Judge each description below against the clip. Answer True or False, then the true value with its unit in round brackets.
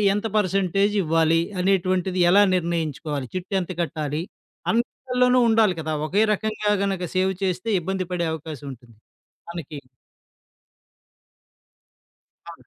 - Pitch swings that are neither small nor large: True (3.5 semitones)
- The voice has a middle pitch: True (180 Hz)